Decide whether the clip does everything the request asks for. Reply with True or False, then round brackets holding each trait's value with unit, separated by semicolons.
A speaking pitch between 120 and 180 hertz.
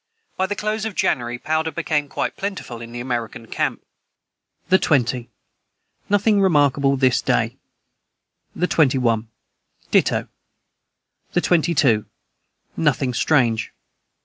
True (140 Hz)